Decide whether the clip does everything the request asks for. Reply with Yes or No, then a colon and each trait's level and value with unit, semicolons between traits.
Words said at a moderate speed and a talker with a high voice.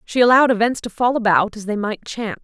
No: fast, 245 wpm; high, 220 Hz